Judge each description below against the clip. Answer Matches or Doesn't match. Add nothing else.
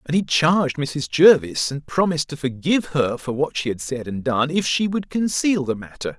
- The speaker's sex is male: Matches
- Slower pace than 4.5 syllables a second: Doesn't match